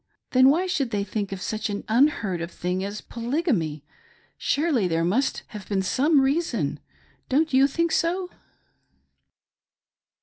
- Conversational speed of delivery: Yes, average, 145 wpm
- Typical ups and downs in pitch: No, wide, 7.2 semitones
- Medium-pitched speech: No, high, 235 Hz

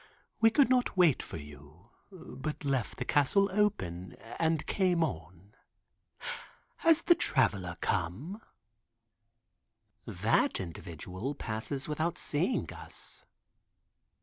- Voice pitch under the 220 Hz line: Yes, medium, 140 Hz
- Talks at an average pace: No, slow, 100 wpm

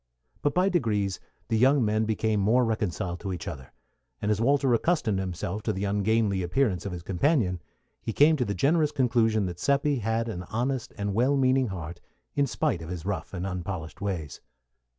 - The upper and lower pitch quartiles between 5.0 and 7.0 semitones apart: Yes, wide, 5.5 semitones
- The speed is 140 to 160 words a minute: No, average, 190 wpm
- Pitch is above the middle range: No, low, 110 Hz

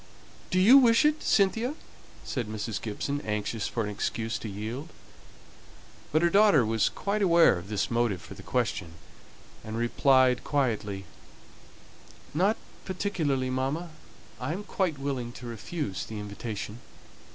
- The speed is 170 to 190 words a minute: No, average, 140 wpm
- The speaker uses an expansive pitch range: Yes, wide, 8.0 semitones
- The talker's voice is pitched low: Yes, low, 125 Hz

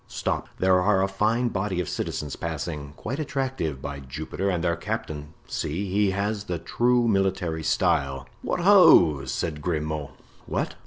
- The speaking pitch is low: Yes, very low, 90 Hz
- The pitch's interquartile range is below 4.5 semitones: No, wide, 5.5 semitones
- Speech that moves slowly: No, average, 150 wpm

